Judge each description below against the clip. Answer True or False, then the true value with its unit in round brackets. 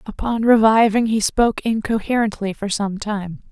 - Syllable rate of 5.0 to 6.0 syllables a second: False (4.8 syllables/s)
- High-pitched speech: True (215 Hz)